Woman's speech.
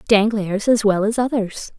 Yes: female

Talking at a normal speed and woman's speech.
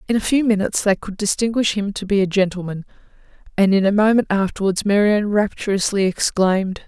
Yes: average, 175 wpm; female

